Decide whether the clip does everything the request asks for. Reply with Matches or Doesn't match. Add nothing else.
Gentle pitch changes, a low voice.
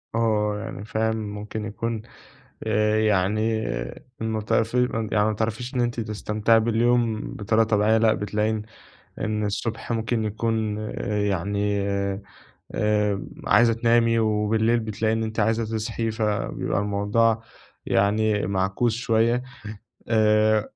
Matches